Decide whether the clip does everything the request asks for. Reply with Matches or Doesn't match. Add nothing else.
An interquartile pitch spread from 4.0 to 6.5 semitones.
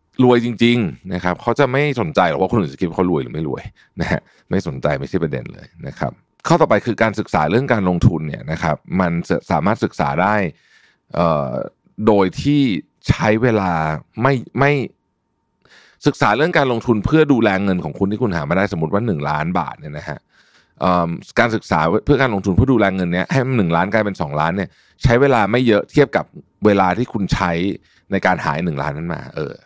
Matches